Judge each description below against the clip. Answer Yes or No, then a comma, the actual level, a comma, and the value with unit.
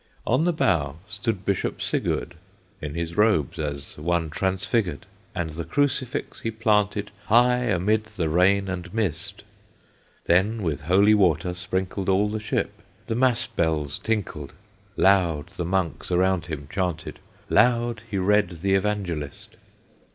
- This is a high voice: No, very low, 95 Hz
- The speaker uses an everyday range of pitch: Yes, average, 4.1 semitones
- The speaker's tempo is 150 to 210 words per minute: No, slow, 135 wpm